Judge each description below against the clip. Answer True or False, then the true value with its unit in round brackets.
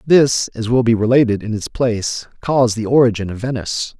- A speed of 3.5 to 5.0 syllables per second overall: False (5.7 syllables/s)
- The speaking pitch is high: False (115 Hz)